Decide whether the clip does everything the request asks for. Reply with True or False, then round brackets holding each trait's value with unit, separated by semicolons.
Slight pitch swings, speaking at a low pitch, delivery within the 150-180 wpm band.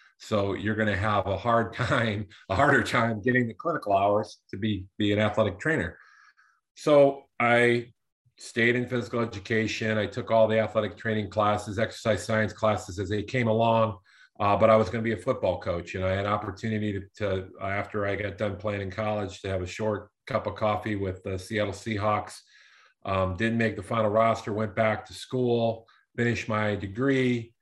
False (2.0 semitones; 110 Hz; 190 wpm)